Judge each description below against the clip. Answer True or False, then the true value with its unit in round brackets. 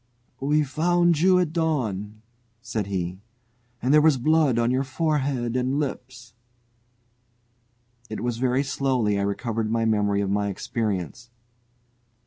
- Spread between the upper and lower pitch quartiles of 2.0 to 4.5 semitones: False (5.2 semitones)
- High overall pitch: False (125 Hz)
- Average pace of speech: False (130 wpm)